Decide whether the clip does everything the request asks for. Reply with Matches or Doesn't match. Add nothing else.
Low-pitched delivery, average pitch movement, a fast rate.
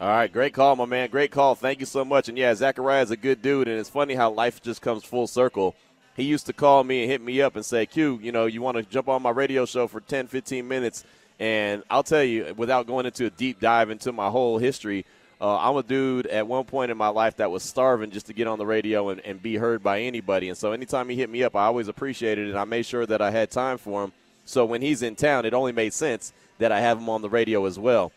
Matches